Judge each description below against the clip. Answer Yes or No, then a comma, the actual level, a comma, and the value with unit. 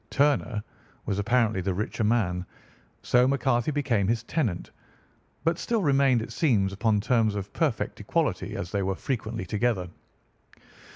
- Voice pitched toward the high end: No, low, 115 Hz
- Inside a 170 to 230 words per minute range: No, average, 140 wpm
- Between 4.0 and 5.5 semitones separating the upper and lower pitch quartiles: Yes, average, 4.8 semitones